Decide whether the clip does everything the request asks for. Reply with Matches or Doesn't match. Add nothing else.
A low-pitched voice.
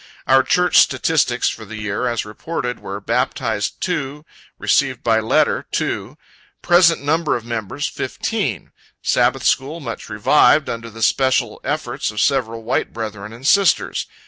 Matches